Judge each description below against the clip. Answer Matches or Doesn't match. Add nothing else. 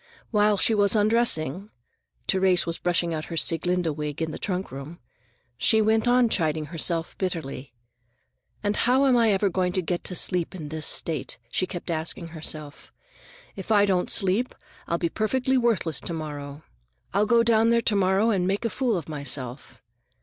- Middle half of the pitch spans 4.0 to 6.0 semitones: Matches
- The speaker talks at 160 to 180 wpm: Matches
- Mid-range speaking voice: Matches